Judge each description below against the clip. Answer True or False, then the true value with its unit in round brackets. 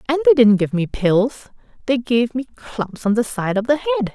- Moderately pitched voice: False (240 Hz)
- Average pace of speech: False (230 wpm)